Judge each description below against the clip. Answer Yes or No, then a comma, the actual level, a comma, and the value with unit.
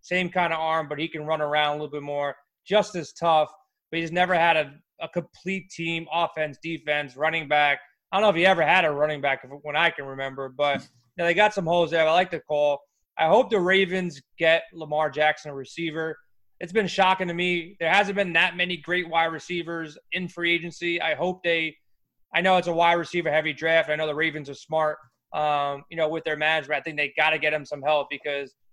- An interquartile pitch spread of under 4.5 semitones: Yes, narrow, 2.6 semitones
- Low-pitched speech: No, medium, 160 Hz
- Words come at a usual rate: No, fast, 235 wpm